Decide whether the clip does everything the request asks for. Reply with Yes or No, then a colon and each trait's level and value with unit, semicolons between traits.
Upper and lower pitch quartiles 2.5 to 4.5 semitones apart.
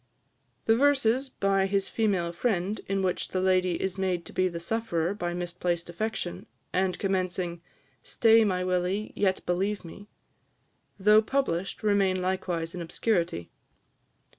Yes: average, 2.9 semitones